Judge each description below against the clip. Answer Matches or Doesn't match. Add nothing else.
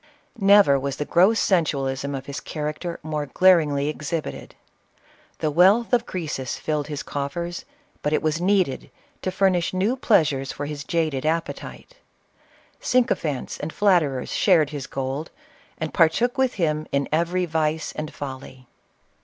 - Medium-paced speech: Matches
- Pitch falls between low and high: Matches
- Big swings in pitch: Doesn't match